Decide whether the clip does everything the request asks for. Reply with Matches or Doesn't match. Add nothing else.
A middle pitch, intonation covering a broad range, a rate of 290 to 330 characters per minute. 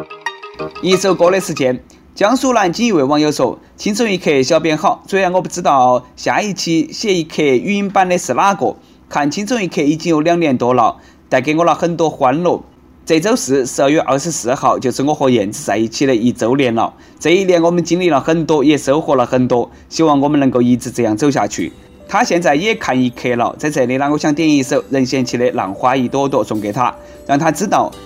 Matches